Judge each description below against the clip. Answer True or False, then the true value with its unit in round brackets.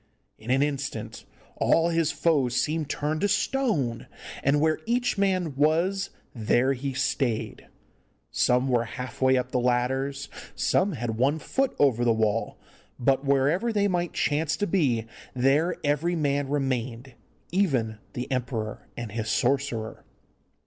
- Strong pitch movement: False (4.6 semitones)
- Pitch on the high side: False (140 Hz)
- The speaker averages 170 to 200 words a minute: False (140 wpm)